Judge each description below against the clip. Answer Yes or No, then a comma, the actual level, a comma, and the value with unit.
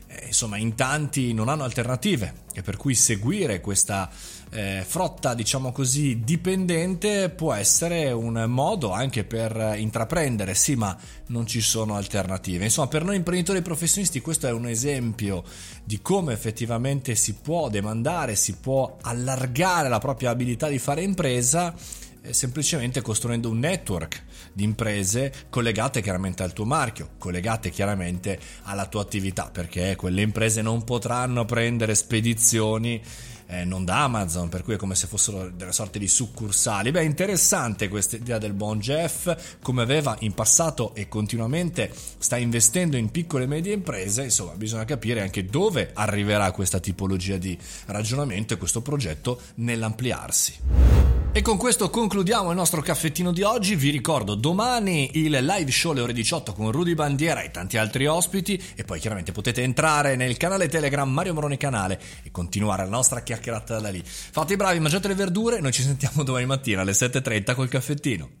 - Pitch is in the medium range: No, low, 120 Hz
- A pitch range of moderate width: No, wide, 6.1 semitones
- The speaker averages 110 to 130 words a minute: No, average, 160 wpm